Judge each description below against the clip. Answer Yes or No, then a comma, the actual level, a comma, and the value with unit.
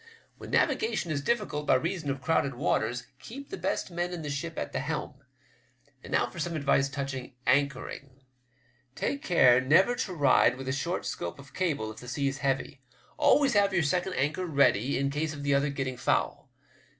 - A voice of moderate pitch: Yes, medium, 145 Hz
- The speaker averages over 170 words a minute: Yes, average, 190 wpm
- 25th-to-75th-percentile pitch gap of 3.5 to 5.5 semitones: Yes, average, 4.3 semitones